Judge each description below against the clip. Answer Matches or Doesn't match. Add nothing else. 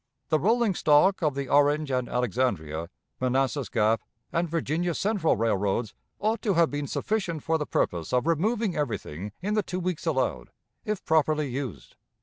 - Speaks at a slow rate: Doesn't match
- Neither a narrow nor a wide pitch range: Doesn't match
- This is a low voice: Doesn't match